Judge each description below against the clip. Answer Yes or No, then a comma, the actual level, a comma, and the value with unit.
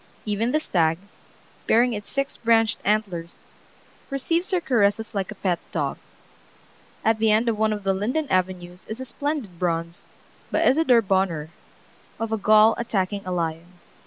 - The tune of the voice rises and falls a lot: No, average, 4.1 semitones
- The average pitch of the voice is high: Yes, high, 215 Hz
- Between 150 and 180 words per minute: Yes, average, 160 wpm